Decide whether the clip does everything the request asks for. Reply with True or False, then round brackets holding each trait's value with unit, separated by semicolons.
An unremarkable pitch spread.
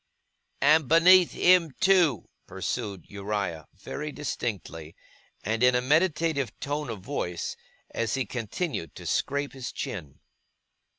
False (7.0 semitones)